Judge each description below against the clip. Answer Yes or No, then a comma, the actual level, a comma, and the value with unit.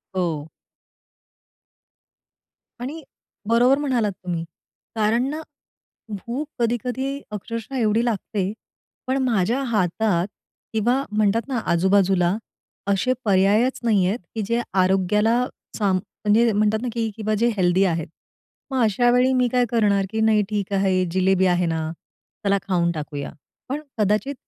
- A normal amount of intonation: Yes, average, 4.1 semitones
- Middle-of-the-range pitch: No, high, 210 Hz